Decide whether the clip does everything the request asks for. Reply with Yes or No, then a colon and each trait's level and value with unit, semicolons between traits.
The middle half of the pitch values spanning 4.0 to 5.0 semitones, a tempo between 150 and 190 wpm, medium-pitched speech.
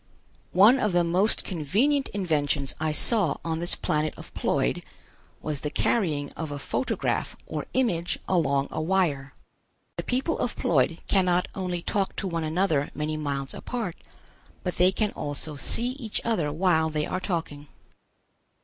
Yes: average, 4.4 semitones; average, 155 wpm; medium, 170 Hz